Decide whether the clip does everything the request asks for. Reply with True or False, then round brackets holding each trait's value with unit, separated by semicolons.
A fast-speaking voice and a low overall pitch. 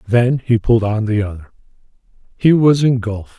False (160 wpm; 115 Hz)